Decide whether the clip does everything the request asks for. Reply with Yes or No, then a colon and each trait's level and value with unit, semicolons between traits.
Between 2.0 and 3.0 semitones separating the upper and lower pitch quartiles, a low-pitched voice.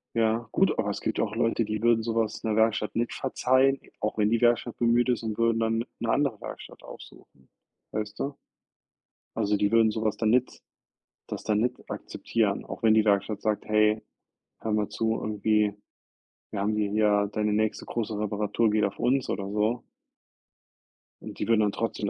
No: narrow, 1.6 semitones; low, 110 Hz